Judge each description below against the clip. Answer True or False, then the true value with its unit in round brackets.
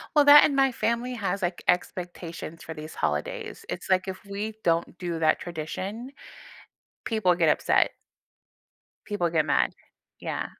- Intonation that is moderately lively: True (4.7 semitones)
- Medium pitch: True (180 Hz)